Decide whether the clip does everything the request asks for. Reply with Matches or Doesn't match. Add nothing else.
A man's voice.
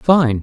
Matches